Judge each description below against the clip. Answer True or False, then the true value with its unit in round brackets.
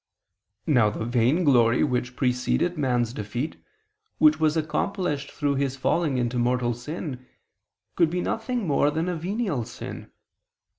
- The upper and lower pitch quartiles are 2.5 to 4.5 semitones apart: False (4.9 semitones)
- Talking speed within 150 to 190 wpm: False (135 wpm)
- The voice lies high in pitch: False (140 Hz)